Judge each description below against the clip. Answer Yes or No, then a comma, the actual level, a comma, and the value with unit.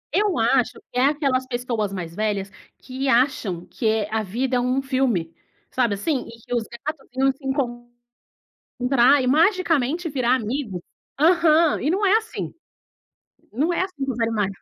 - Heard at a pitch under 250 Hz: No, very high, 255 Hz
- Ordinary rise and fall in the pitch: Yes, average, 4.2 semitones